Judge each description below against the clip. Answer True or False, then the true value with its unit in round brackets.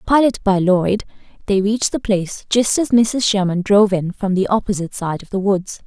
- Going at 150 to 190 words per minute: False (205 wpm)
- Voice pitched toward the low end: False (200 Hz)